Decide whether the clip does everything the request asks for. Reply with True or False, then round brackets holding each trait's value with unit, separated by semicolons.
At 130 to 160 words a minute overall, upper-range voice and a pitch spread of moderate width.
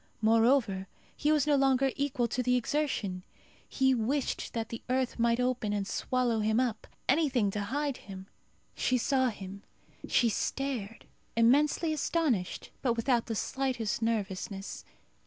True (140 wpm; 245 Hz; 3.7 semitones)